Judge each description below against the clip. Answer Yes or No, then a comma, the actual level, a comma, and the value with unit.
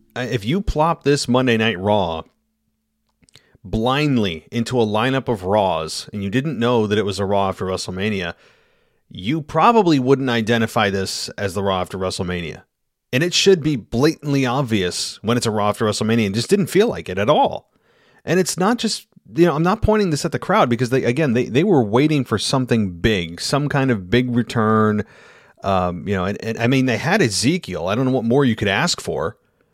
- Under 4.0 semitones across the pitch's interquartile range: No, wide, 5.4 semitones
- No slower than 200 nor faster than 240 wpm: Yes, fast, 205 wpm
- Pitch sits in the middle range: No, low, 120 Hz